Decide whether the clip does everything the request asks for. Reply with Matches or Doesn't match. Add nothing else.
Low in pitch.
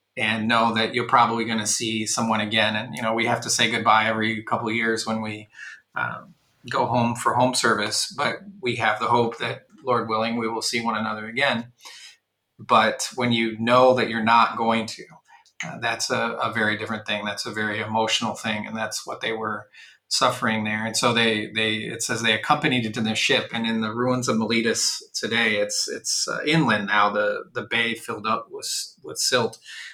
Matches